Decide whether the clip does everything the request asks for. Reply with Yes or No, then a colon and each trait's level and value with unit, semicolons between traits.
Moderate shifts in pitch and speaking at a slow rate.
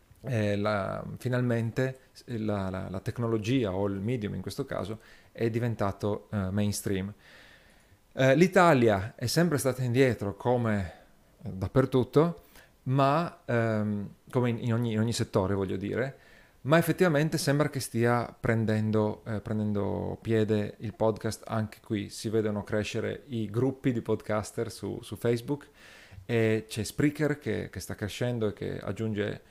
No: average, 3.4 semitones; average, 140 wpm